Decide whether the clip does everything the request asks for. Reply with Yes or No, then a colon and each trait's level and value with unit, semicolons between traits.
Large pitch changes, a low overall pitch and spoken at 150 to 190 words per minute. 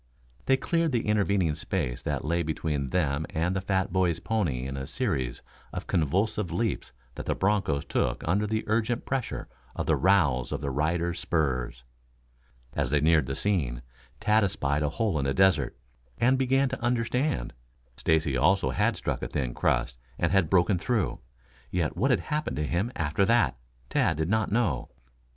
Yes: wide, 6.8 semitones; very low, 85 Hz; average, 175 wpm